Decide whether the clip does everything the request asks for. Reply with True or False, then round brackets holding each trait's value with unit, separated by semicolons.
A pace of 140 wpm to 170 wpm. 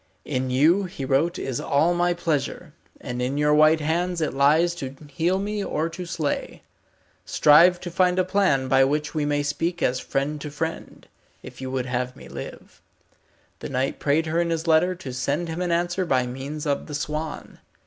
False (195 wpm)